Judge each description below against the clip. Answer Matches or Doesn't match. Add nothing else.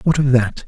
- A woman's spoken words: Doesn't match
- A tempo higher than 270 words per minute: Doesn't match